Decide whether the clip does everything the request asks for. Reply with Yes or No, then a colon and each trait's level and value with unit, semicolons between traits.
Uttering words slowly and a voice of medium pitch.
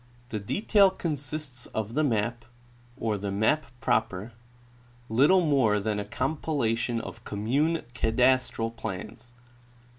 No: slow, 115 wpm; low, 120 Hz